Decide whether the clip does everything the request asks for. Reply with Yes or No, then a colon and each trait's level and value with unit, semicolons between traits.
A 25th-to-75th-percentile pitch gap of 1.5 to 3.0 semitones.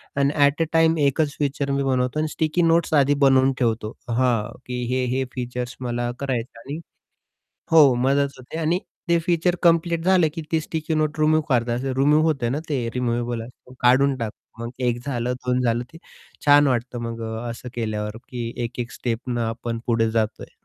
No: average, 4.2 semitones